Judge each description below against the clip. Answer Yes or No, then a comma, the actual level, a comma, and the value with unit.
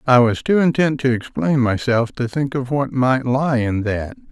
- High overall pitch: No, low, 130 Hz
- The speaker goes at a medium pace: No, fast, 210 wpm